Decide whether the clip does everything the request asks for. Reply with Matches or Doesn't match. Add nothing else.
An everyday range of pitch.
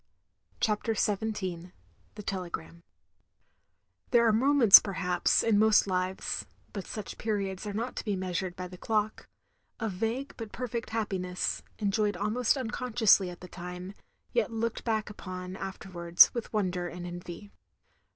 Matches